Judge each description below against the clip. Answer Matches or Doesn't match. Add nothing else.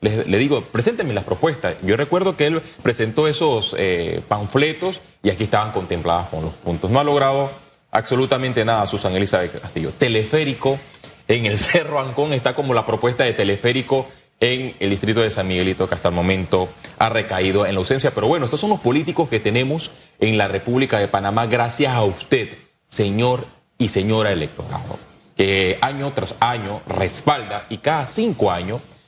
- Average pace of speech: Matches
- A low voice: Matches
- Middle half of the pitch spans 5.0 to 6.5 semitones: Matches